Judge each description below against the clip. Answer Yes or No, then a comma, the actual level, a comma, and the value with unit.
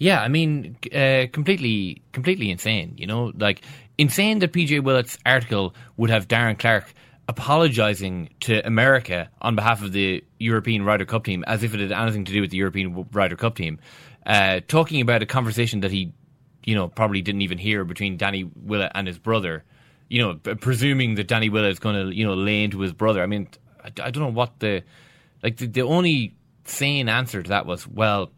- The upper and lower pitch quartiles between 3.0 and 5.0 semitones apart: Yes, average, 4.5 semitones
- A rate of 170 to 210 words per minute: Yes, average, 200 wpm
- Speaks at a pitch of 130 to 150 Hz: No, low, 110 Hz